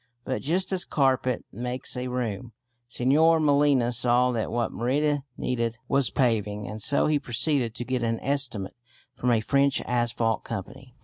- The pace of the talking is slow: No, average, 165 wpm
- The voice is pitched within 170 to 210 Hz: No, low, 125 Hz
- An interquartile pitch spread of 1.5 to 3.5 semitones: Yes, average, 3.0 semitones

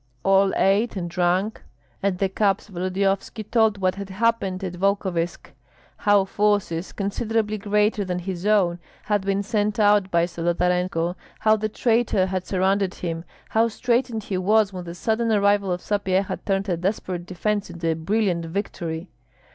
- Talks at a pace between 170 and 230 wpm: No, average, 155 wpm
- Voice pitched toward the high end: Yes, high, 195 Hz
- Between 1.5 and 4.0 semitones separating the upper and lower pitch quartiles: Yes, narrow, 2.6 semitones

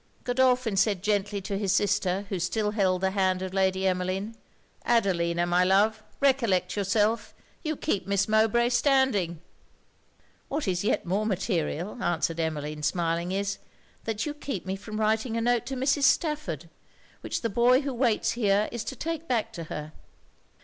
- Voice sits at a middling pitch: No, high, 205 Hz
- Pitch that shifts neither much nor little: Yes, average, 4.3 semitones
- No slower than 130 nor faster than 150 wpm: No, average, 160 wpm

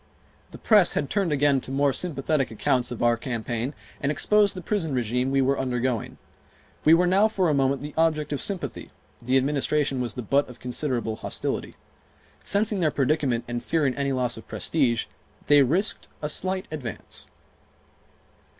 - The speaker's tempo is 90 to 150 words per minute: No, average, 170 wpm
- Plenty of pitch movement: No, average, 4.3 semitones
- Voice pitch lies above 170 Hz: No, medium, 140 Hz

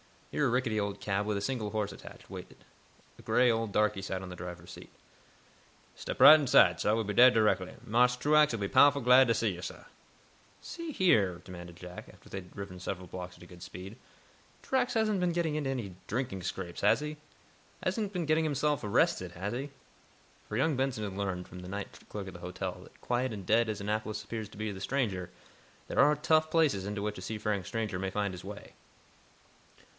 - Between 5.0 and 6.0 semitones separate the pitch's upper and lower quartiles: Yes, wide, 5.6 semitones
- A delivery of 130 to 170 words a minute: No, fast, 205 wpm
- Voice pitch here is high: No, low, 105 Hz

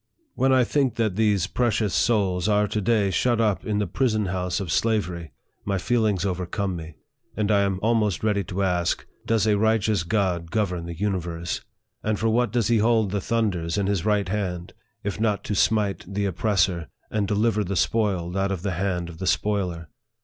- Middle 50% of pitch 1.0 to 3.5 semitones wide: Yes, average, 3.2 semitones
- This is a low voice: Yes, low, 100 Hz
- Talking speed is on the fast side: Yes, fast, 210 wpm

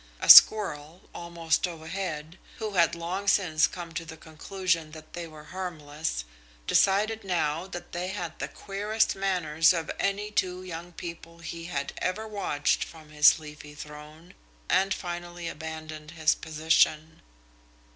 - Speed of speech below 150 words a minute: Yes, average, 140 wpm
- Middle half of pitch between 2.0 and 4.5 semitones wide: Yes, average, 2.8 semitones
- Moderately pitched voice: Yes, medium, 170 Hz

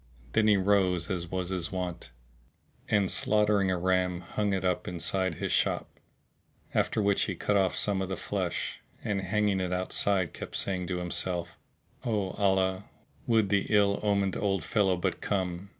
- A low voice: Yes, very low, 95 Hz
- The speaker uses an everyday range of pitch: No, narrow, 1.9 semitones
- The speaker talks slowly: No, average, 165 wpm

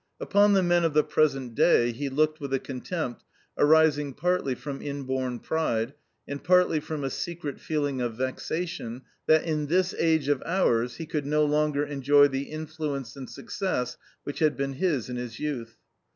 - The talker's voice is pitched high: No, medium, 145 Hz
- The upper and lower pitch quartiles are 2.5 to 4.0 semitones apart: Yes, average, 3.1 semitones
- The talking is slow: No, average, 175 wpm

